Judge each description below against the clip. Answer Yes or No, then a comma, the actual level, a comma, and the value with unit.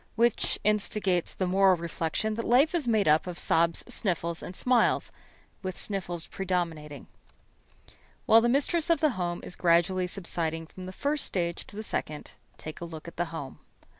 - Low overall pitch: No, medium, 185 Hz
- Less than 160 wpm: No, average, 170 wpm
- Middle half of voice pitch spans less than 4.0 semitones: No, average, 4.5 semitones